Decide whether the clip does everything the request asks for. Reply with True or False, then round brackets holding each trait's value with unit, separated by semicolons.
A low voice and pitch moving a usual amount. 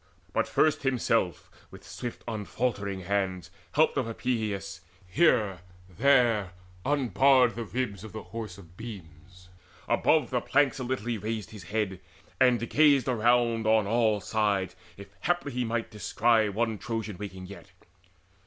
True (110 Hz; 3.8 semitones)